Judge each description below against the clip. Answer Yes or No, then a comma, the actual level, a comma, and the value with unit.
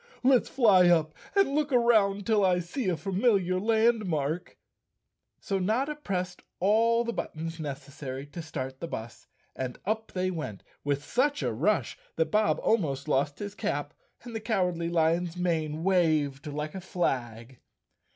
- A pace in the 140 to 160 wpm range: Yes, average, 155 wpm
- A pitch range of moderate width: No, wide, 6.1 semitones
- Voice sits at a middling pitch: Yes, medium, 180 Hz